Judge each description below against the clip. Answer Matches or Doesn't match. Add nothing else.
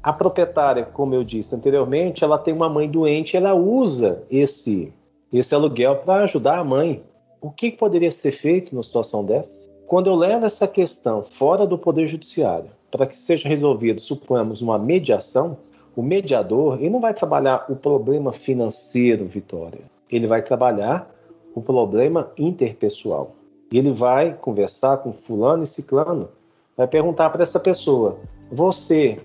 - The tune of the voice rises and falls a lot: Matches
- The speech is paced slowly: Doesn't match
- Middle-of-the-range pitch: Matches